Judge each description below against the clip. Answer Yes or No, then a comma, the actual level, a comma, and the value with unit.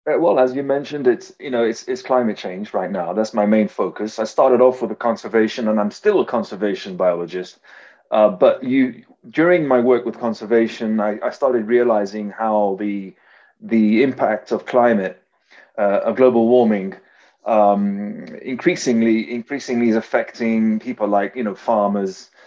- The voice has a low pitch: Yes, low, 115 Hz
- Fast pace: No, average, 165 wpm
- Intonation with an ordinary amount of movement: Yes, average, 3.4 semitones